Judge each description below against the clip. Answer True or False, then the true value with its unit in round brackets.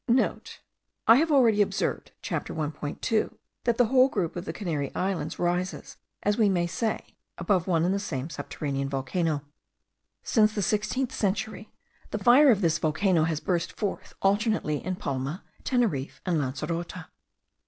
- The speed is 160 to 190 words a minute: False (150 wpm)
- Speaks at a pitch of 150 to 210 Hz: True (185 Hz)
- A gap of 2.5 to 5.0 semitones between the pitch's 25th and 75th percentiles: False (5.5 semitones)